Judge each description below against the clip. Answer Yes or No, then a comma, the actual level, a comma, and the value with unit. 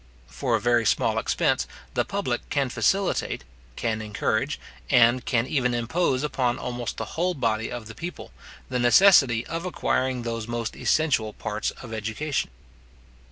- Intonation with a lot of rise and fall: No, average, 3.3 semitones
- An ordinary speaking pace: Yes, average, 150 wpm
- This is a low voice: Yes, low, 120 Hz